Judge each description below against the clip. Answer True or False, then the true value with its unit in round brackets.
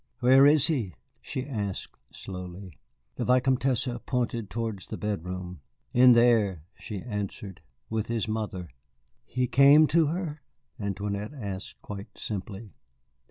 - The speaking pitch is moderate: False (110 Hz)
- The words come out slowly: True (120 wpm)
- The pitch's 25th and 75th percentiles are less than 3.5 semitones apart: False (4.5 semitones)